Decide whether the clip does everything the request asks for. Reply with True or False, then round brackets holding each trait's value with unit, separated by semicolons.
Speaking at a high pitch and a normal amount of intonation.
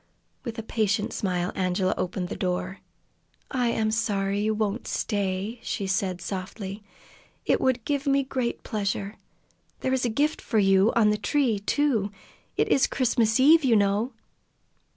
True (215 Hz; 3.8 semitones)